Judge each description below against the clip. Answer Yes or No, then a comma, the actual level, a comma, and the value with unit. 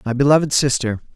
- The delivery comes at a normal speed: Yes, average, 155 wpm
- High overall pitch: No, low, 135 Hz